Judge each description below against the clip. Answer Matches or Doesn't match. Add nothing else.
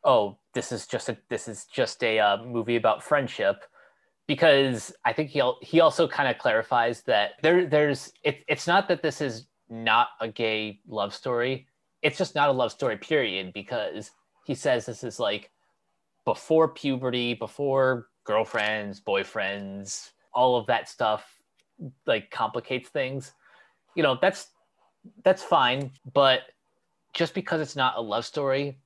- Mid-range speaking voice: Doesn't match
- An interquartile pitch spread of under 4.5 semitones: Doesn't match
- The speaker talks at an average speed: Matches